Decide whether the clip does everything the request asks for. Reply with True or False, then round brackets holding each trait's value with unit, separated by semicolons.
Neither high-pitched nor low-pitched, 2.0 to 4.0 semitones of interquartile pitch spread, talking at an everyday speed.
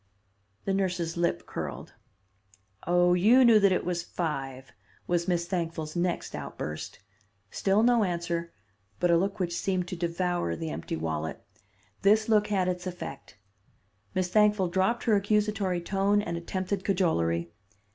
True (180 Hz; 2.7 semitones; 145 wpm)